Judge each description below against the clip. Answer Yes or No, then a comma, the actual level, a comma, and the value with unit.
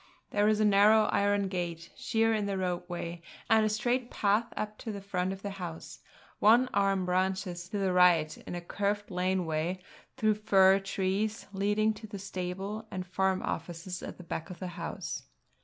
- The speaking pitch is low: No, high, 195 Hz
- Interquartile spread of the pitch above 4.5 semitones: No, average, 2.7 semitones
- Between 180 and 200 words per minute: Yes, average, 185 wpm